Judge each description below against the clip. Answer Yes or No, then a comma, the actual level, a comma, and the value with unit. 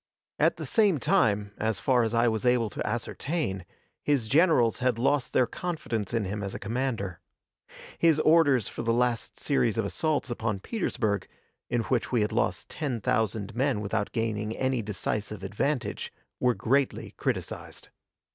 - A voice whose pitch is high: No, low, 115 Hz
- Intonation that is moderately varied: Yes, average, 3.9 semitones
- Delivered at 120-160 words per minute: Yes, average, 155 wpm